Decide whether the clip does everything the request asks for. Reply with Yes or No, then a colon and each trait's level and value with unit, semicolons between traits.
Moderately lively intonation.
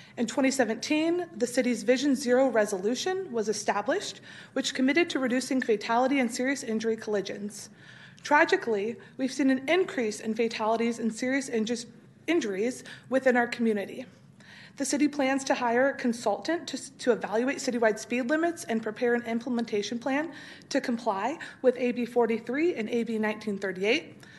Yes: average, 3.3 semitones